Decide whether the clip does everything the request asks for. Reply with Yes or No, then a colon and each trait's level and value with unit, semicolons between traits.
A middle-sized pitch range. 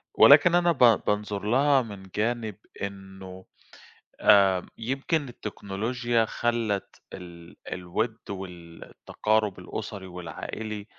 Yes: average, 3.6 semitones